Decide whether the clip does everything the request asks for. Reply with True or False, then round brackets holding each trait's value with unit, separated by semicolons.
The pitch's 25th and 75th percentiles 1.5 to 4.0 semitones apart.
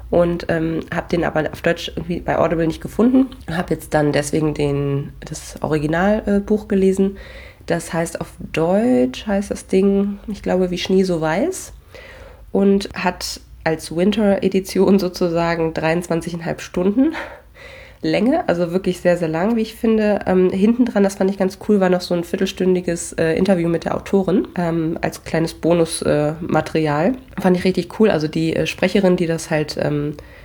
True (3.4 semitones)